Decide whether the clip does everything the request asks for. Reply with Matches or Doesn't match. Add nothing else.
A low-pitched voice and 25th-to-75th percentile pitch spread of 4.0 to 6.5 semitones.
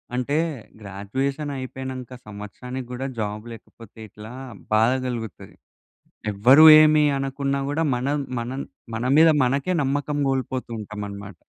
Matches